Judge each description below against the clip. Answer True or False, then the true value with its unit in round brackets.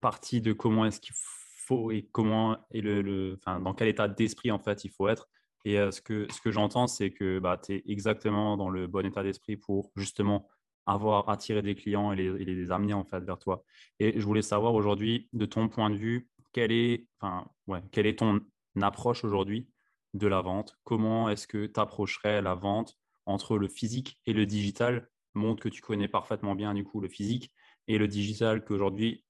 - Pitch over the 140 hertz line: False (105 Hz)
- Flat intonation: True (1.9 semitones)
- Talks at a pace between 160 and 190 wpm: False (210 wpm)